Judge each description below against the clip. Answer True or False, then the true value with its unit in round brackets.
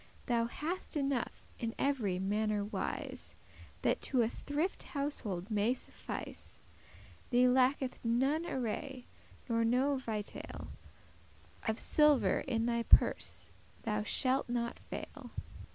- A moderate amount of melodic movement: True (3.5 semitones)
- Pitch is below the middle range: False (245 Hz)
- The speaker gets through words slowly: True (115 wpm)